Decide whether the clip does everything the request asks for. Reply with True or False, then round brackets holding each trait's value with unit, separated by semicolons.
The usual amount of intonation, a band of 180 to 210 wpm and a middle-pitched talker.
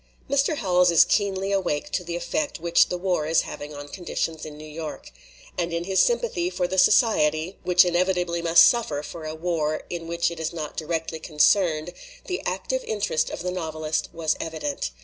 True (3.3 semitones; 190 wpm; 170 Hz)